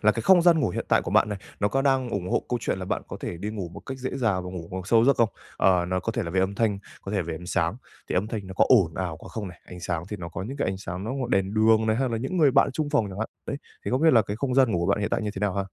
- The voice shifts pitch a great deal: No, average, 4.7 semitones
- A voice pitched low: Yes, low, 105 Hz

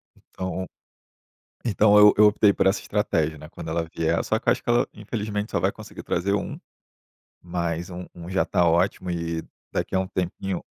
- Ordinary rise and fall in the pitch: Yes, average, 3.3 semitones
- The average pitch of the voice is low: Yes, very low, 95 Hz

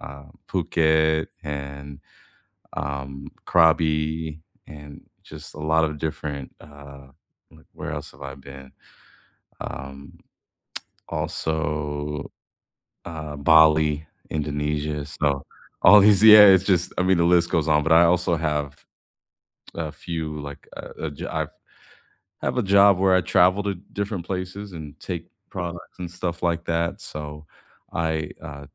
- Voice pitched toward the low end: Yes, very low, 80 Hz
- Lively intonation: No, average, 2.9 semitones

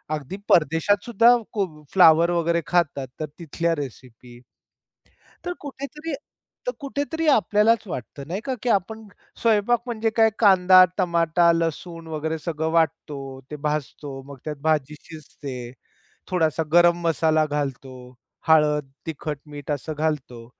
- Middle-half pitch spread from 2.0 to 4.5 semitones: No, average, 4.9 semitones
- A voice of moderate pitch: Yes, medium, 165 Hz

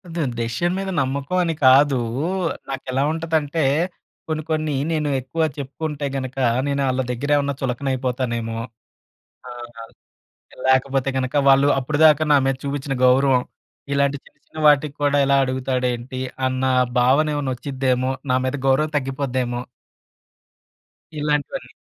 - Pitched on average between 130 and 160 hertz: Yes, low, 135 Hz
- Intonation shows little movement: Yes, narrow, 2.2 semitones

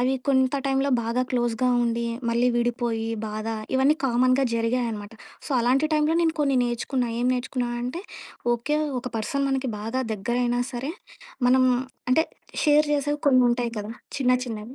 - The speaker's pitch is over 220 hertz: Yes, very high, 250 Hz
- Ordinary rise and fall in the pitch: No, narrow, 2.3 semitones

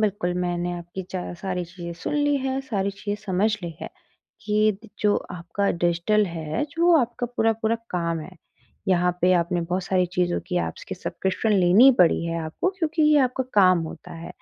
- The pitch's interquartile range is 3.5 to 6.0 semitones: Yes, average, 3.8 semitones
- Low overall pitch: No, medium, 185 Hz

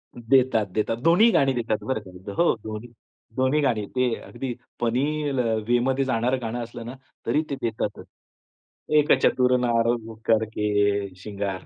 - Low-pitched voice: Yes, low, 120 Hz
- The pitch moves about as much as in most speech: Yes, average, 3.2 semitones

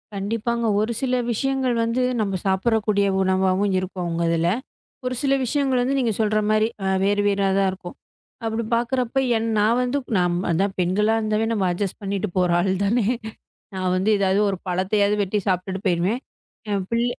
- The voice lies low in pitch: No, high, 205 Hz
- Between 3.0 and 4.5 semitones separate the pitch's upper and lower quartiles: Yes, average, 3.6 semitones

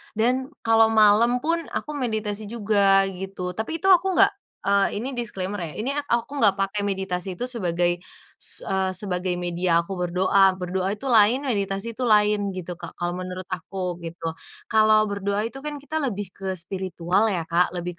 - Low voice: No, high, 200 Hz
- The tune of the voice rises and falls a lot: No, average, 3.8 semitones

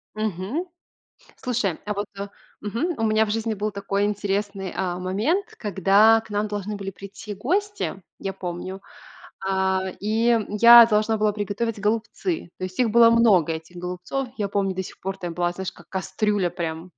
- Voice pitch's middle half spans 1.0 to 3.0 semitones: Yes, average, 2.7 semitones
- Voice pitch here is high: Yes, high, 205 Hz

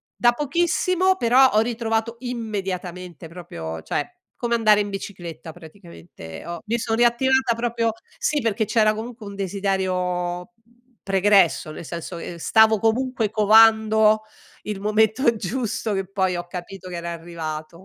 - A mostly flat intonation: No, average, 4.6 semitones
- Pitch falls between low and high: No, high, 210 Hz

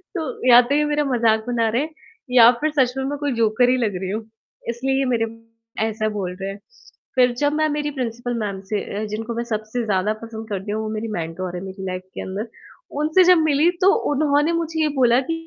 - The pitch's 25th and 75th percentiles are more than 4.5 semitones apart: Yes, average, 5.0 semitones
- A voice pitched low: No, high, 235 Hz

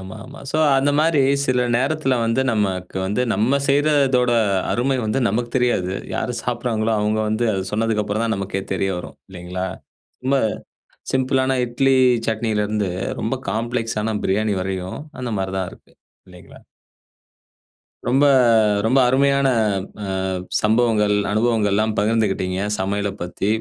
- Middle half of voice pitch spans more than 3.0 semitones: Yes, average, 3.9 semitones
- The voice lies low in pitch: Yes, low, 110 Hz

